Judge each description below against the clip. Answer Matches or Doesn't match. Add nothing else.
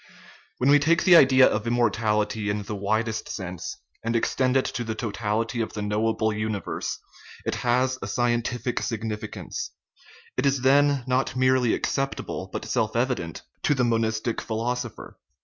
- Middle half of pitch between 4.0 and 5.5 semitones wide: Doesn't match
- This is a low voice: Matches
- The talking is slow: Doesn't match